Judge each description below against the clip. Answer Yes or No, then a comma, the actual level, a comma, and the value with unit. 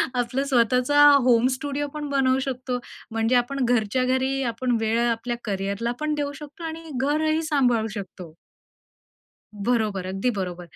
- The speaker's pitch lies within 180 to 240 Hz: No, very high, 250 Hz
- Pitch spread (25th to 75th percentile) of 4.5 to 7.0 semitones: No, average, 3.8 semitones